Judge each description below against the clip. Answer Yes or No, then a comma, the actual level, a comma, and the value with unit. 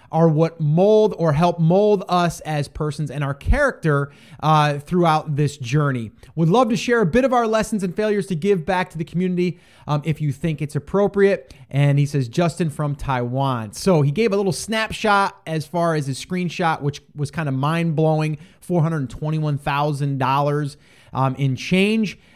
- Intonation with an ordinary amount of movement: Yes, average, 4.2 semitones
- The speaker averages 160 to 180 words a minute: Yes, average, 175 wpm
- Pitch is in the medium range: Yes, medium, 155 Hz